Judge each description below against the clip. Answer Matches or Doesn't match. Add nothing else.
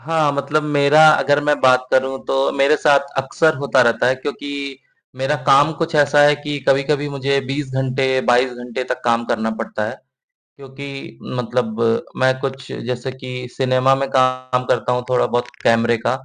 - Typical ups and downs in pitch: Doesn't match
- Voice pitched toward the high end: Doesn't match